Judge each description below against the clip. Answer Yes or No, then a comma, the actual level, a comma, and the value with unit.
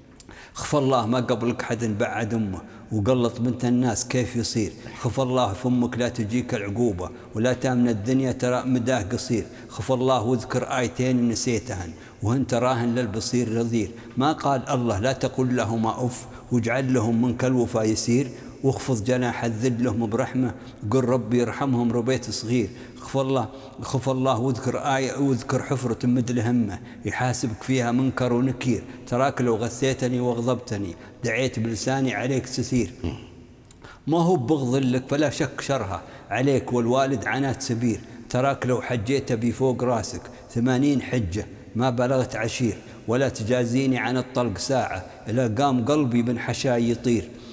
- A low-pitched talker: Yes, low, 125 Hz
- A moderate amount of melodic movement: No, narrow, 1.8 semitones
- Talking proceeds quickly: Yes, fast, 140 wpm